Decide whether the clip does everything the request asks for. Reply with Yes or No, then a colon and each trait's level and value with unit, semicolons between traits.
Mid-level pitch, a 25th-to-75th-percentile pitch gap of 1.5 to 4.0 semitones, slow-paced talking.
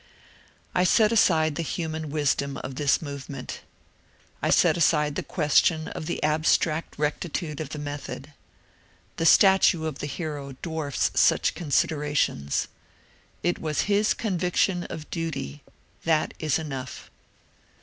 Yes: medium, 155 Hz; narrow, 2.4 semitones; slow, 130 wpm